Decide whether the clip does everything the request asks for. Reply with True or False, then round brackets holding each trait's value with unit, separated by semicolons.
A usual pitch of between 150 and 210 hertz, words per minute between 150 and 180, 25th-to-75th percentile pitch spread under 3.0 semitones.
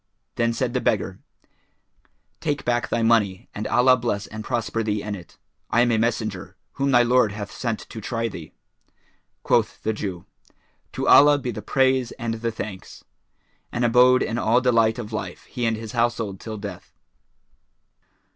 False (115 Hz; 170 wpm; 2.4 semitones)